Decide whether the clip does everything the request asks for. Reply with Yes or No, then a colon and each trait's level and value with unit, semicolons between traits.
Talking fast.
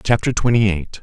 No: average, 175 wpm